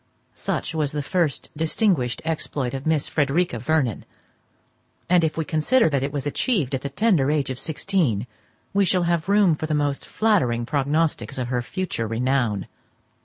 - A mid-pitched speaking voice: Yes, medium, 150 Hz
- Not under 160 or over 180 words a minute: Yes, average, 170 wpm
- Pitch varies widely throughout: No, average, 4.5 semitones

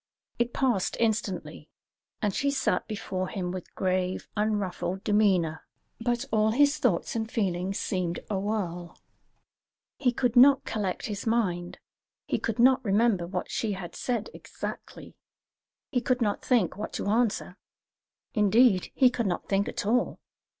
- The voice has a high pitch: Yes, high, 210 Hz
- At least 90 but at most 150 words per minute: Yes, average, 145 wpm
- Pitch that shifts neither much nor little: Yes, average, 4.3 semitones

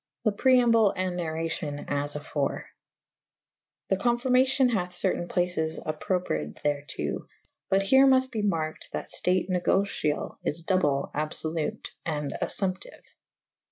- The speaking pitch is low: No, medium, 180 Hz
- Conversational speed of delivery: No, slow, 125 wpm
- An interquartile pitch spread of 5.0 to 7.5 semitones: Yes, wide, 5.4 semitones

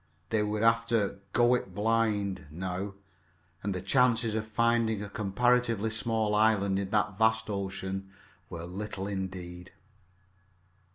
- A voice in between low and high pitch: No, low, 105 Hz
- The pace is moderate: No, slow, 130 wpm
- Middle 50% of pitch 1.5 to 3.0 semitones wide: Yes, average, 2.7 semitones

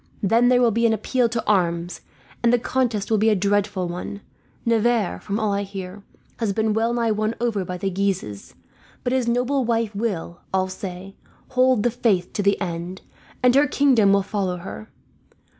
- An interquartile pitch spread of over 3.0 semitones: Yes, average, 3.6 semitones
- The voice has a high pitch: Yes, high, 210 Hz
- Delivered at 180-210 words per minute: Yes, average, 190 wpm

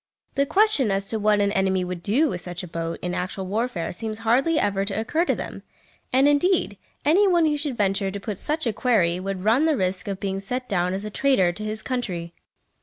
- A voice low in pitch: No, high, 210 Hz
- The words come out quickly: Yes, fast, 230 wpm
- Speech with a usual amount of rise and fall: No, wide, 5.7 semitones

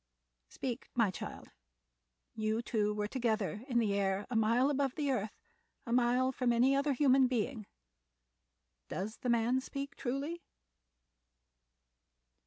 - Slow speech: Yes, slow, 130 wpm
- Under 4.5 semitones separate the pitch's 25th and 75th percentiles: Yes, average, 3.5 semitones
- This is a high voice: Yes, high, 240 Hz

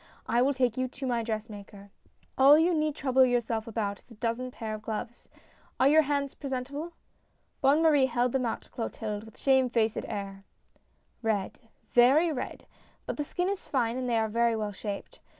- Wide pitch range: No, average, 3.6 semitones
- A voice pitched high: Yes, high, 245 Hz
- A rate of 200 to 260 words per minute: Yes, fast, 205 wpm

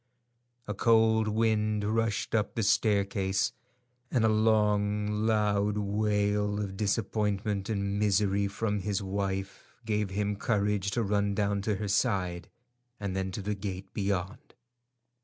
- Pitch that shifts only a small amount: Yes, narrow, 1.3 semitones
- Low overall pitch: Yes, low, 105 Hz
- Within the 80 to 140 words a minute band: Yes, slow, 135 wpm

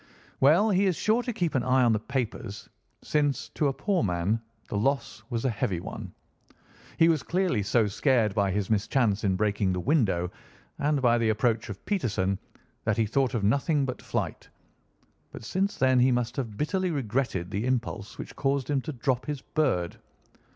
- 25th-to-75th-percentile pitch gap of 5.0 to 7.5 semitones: Yes, wide, 5.5 semitones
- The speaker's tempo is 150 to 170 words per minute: No, average, 185 wpm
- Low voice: Yes, low, 125 Hz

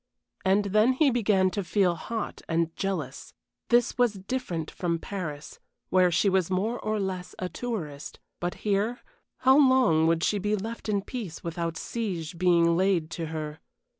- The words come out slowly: No, average, 165 wpm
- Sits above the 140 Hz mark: Yes, high, 190 Hz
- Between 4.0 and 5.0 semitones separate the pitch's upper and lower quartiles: Yes, average, 4.3 semitones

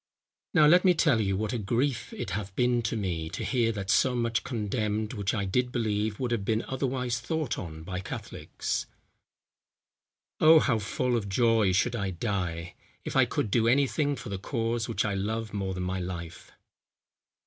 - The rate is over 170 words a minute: Yes, average, 190 wpm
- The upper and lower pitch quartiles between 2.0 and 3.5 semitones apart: No, average, 4.0 semitones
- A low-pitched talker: Yes, low, 110 Hz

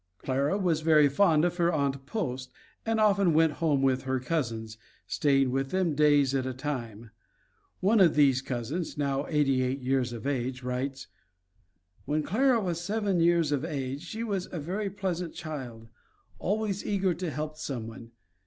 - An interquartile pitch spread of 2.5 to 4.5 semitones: No, average, 5.0 semitones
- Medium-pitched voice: Yes, medium, 150 Hz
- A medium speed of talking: Yes, average, 165 wpm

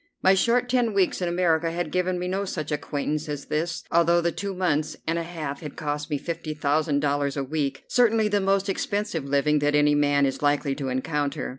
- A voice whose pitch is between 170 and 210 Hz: No, medium, 160 Hz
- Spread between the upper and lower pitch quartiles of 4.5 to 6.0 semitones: No, average, 3.8 semitones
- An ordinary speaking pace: No, fast, 210 wpm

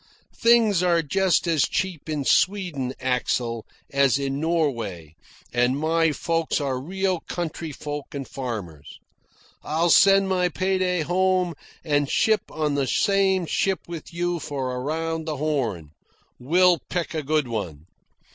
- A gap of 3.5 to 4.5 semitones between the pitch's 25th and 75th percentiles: No, average, 5.0 semitones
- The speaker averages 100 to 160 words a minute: Yes, average, 140 wpm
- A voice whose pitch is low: No, medium, 155 Hz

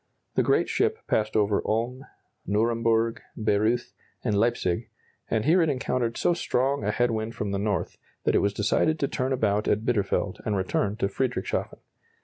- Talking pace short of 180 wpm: Yes, average, 170 wpm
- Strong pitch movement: No, average, 3.0 semitones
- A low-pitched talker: Yes, low, 110 Hz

